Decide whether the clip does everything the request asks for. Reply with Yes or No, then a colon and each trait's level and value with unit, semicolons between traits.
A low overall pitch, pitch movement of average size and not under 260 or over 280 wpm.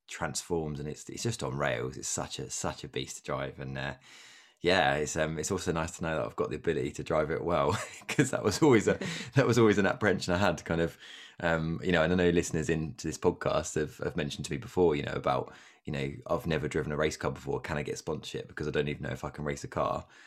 Yes: very low, 80 Hz; average, 3.0 semitones; fast, 270 wpm